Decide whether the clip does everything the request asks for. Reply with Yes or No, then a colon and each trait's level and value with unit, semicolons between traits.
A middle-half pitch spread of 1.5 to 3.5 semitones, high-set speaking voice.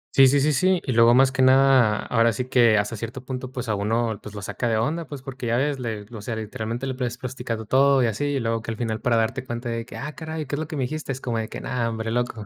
No: average, 2.9 semitones; low, 120 Hz